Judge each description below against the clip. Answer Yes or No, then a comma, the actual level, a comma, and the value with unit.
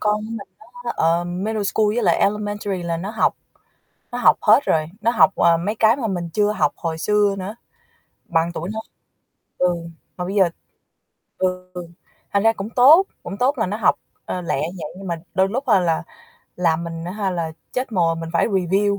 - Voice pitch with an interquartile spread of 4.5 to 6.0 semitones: No, average, 3.7 semitones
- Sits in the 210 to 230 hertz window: No, high, 195 Hz